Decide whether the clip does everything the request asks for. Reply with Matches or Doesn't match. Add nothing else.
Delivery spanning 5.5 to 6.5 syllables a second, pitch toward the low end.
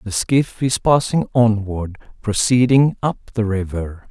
Doesn't match